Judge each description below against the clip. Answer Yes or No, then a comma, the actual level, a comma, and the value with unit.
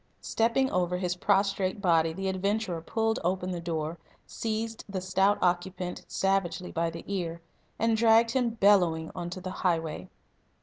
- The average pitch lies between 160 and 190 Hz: Yes, medium, 185 Hz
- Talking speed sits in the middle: Yes, average, 150 wpm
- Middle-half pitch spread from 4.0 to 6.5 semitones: No, average, 3.0 semitones